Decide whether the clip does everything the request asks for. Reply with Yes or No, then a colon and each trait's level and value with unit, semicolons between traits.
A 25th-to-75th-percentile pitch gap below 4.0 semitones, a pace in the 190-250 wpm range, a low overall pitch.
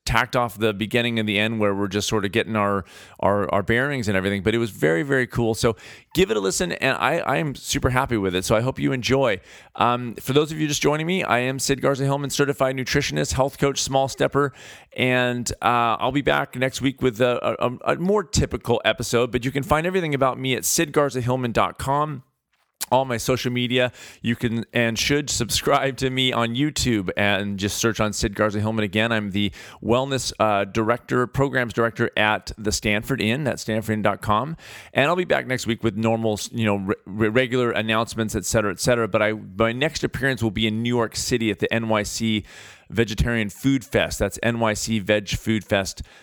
Yes: average, 3.3 semitones; fast, 205 wpm; low, 115 Hz